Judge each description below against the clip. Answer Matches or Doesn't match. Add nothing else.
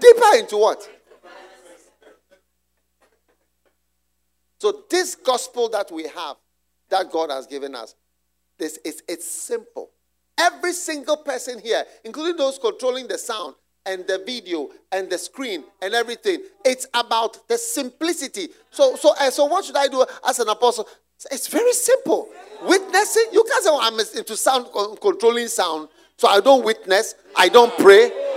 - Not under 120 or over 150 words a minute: Matches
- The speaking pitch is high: Matches